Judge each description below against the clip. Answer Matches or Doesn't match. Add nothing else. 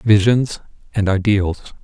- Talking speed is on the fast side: Doesn't match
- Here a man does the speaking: Matches